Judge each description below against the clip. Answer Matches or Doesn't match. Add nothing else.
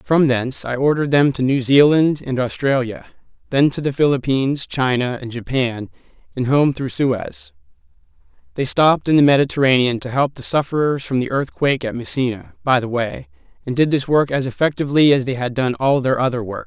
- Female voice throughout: Doesn't match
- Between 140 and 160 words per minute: Doesn't match